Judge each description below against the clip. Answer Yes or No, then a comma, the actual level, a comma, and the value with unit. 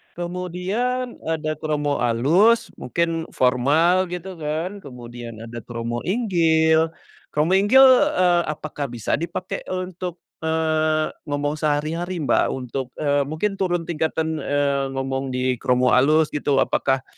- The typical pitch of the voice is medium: Yes, medium, 155 Hz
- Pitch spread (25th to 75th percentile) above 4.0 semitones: Yes, average, 4.5 semitones